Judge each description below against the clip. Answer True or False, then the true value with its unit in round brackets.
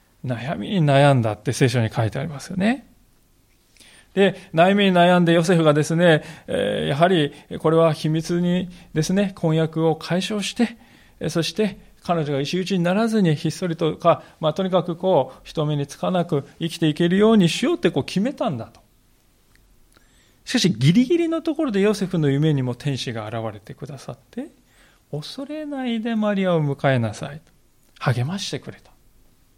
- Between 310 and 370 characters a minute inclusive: True (325 characters per minute)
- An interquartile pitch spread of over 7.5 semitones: False (5.3 semitones)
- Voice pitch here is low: False (170 Hz)